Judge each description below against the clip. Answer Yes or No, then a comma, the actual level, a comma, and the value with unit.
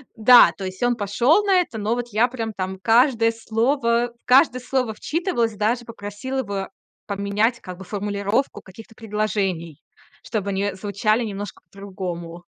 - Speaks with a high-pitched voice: Yes, high, 215 Hz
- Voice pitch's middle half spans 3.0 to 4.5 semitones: Yes, average, 3.3 semitones